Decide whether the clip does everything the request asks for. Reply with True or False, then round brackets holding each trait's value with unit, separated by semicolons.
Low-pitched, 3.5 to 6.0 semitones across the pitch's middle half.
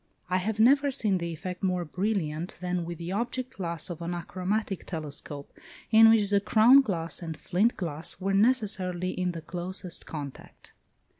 False (185 Hz; 3.9 semitones)